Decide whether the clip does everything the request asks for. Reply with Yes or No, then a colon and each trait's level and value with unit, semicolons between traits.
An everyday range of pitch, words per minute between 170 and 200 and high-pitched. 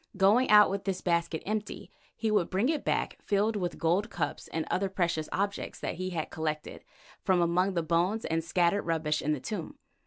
No: average, 3.6 semitones; average, 195 wpm; medium, 180 Hz